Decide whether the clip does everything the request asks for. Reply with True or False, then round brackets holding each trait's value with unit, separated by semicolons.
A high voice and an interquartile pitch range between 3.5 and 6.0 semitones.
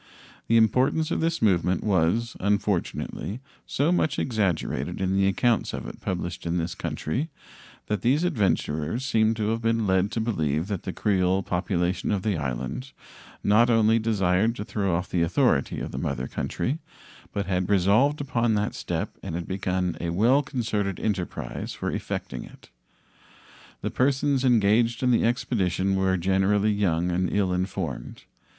False (100 Hz; 4.3 semitones)